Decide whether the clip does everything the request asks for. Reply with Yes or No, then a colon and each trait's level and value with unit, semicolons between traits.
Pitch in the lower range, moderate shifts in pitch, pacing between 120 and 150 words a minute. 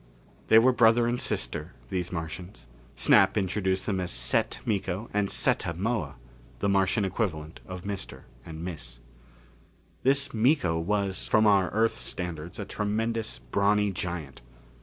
Yes: very low, 95 Hz; average, 3.9 semitones; average, 140 wpm